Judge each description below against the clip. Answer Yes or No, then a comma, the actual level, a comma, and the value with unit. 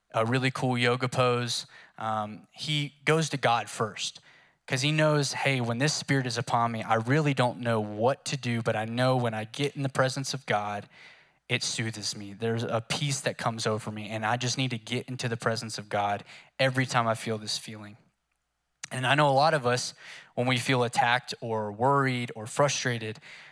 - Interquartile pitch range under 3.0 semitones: No, average, 3.3 semitones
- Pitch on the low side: Yes, low, 125 Hz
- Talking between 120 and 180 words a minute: No, fast, 205 wpm